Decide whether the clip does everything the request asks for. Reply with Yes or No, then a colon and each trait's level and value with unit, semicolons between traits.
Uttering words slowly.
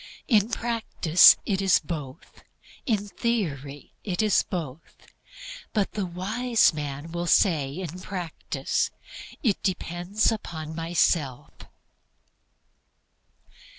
Yes: slow, 95 wpm